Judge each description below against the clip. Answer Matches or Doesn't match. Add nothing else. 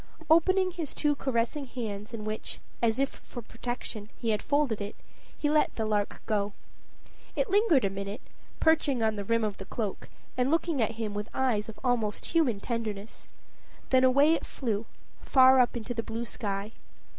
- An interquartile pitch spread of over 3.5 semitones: Matches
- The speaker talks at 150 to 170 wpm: Doesn't match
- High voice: Matches